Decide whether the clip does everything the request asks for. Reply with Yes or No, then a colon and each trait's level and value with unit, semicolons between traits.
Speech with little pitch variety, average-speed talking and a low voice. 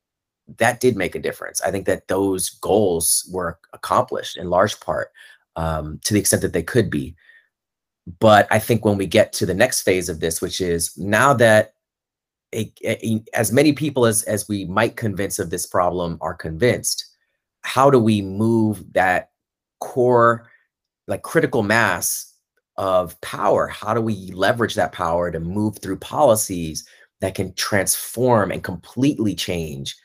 No: average, 4.3 semitones; average, 160 wpm; low, 100 Hz